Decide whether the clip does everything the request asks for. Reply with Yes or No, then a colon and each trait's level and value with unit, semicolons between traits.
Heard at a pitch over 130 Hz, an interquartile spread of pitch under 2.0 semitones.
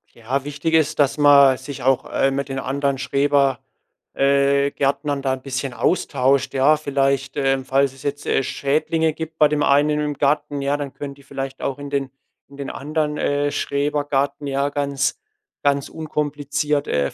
Yes: medium, 140 Hz; narrow, 1.2 semitones